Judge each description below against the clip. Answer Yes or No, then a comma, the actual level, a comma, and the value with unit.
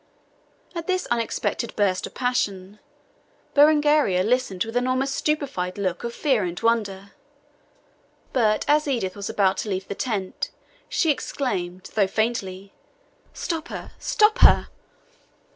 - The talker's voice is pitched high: Yes, high, 225 Hz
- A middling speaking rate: No, slow, 130 wpm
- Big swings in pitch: Yes, wide, 6.1 semitones